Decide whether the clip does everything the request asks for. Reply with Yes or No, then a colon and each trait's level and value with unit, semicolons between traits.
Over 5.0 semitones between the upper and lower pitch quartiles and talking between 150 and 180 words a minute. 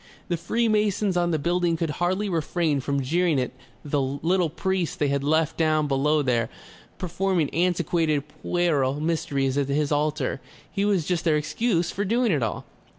No: average, 3.6 semitones; average, 165 wpm